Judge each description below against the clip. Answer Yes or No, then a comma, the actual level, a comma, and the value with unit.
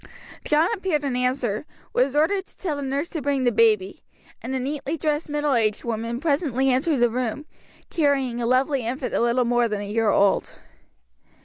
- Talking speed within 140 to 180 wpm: No, average, 190 wpm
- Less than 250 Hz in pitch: No, very high, 260 Hz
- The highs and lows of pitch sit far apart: No, average, 3.8 semitones